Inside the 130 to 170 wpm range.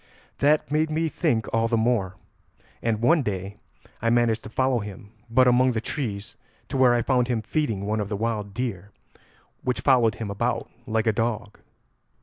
No: average, 180 wpm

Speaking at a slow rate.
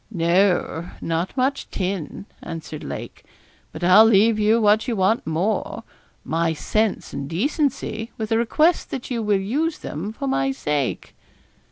No: average, 150 wpm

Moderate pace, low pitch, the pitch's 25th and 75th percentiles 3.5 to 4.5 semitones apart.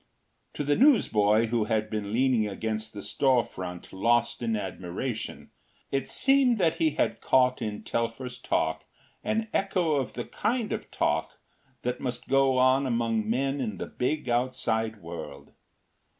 Yes: average, 150 wpm; low, 120 Hz; average, 3.8 semitones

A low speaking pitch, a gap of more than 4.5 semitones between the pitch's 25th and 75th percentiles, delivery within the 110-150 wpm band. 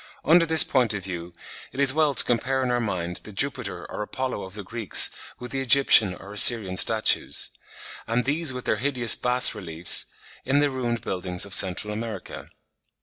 No: low, 115 Hz; average, 5.1 semitones; average, 185 wpm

